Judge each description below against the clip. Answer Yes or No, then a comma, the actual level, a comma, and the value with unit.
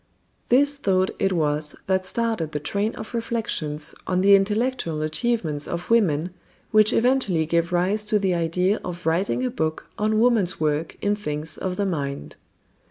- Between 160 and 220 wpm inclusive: Yes, average, 165 wpm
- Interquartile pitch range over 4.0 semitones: Yes, average, 5.2 semitones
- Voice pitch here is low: No, medium, 185 Hz